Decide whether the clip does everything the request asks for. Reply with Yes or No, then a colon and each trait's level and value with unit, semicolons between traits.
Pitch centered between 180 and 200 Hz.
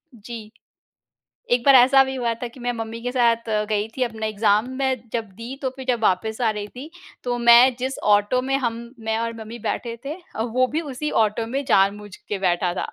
No: high, 230 Hz